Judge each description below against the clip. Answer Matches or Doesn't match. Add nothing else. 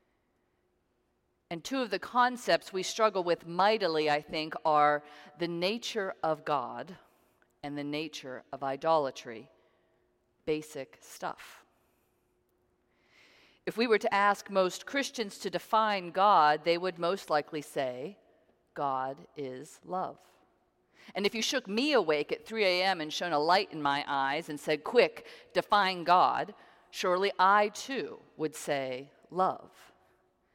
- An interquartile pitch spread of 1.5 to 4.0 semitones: Doesn't match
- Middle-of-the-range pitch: Matches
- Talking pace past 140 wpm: Doesn't match